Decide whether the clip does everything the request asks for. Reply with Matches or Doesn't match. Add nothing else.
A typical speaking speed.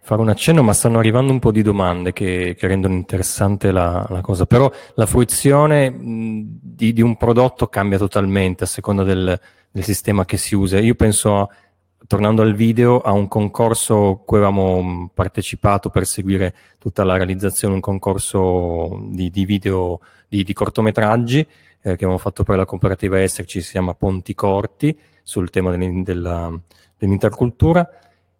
Matches